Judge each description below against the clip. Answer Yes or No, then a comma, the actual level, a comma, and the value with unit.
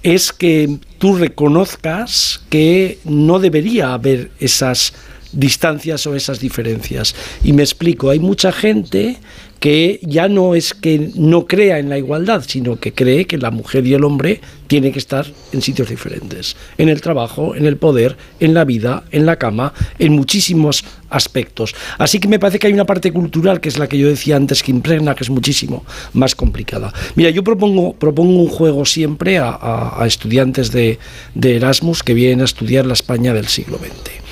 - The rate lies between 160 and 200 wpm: Yes, average, 185 wpm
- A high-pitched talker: No, medium, 145 Hz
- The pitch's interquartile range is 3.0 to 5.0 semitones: Yes, average, 4.7 semitones